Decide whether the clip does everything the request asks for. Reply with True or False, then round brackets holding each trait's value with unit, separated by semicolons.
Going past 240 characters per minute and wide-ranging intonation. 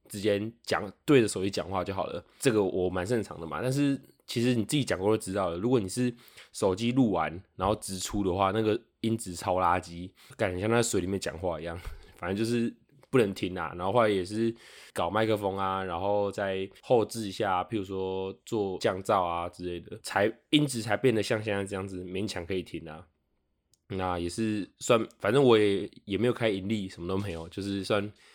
False (300 characters per minute; 3.5 semitones)